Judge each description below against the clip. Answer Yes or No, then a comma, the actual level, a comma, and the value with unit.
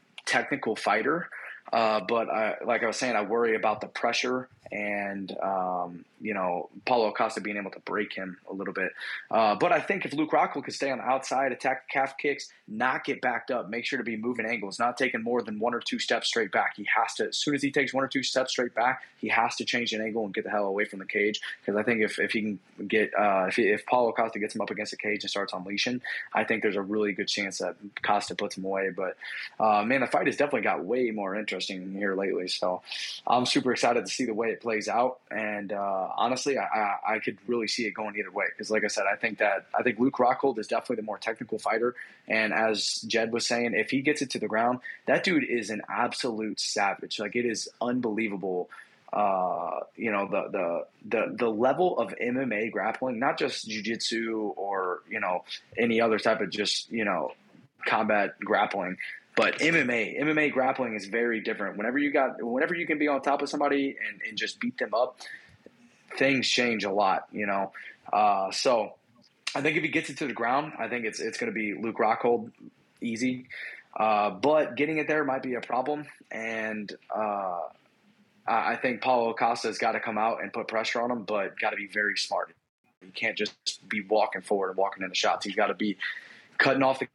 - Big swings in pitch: No, average, 3.6 semitones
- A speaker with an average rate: No, fast, 225 wpm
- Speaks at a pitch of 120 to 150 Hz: No, low, 110 Hz